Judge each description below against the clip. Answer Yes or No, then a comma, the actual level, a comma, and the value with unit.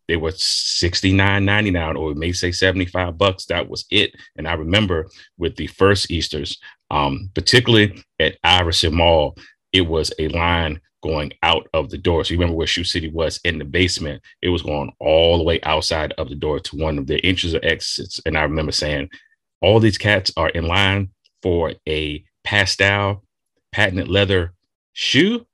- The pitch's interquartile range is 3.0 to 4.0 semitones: Yes, average, 3.4 semitones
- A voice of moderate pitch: No, very low, 90 Hz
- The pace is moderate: Yes, average, 180 wpm